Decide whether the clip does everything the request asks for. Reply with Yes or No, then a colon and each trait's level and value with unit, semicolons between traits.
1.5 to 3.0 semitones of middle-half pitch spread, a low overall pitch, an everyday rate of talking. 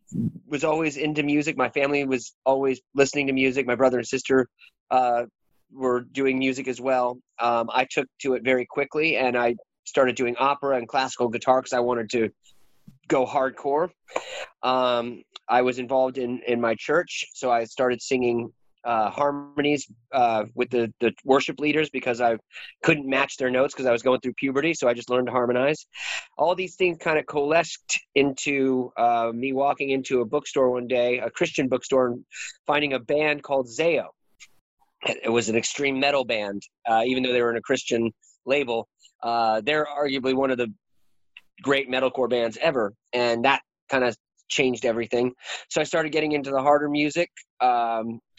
Yes: average, 2.7 semitones; low, 130 Hz; average, 180 wpm